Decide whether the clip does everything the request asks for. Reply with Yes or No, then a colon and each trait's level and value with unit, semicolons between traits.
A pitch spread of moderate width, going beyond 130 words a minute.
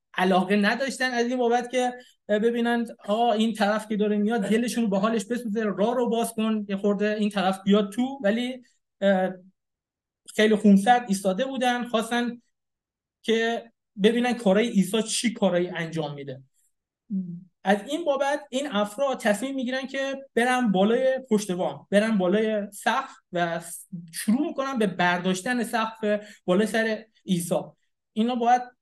Yes: average, 3.7 semitones; average, 140 wpm